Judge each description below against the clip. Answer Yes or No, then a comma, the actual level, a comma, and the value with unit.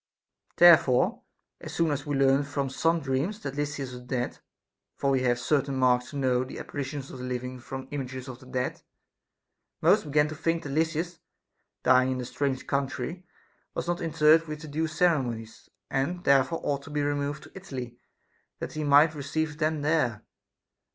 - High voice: No, medium, 140 Hz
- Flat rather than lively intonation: No, average, 3.2 semitones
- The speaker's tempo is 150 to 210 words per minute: Yes, average, 180 wpm